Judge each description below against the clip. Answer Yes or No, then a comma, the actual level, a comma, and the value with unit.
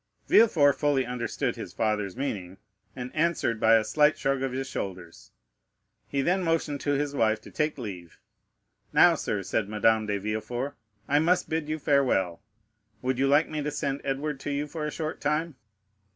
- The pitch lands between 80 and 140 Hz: Yes, low, 135 Hz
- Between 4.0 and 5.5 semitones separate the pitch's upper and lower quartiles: Yes, average, 5.2 semitones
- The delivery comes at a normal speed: Yes, average, 180 wpm